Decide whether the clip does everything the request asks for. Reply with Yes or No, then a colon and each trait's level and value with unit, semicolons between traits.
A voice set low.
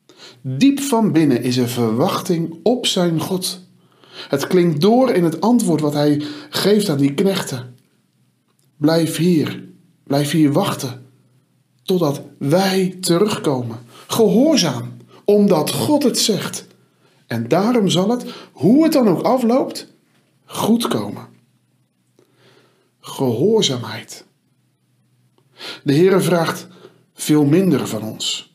No: medium, 165 Hz